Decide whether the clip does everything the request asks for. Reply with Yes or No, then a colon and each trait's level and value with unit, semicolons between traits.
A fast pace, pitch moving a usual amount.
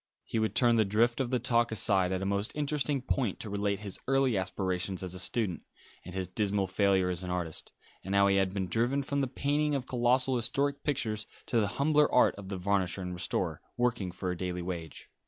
Yes: fast, 220 wpm; average, 5.0 semitones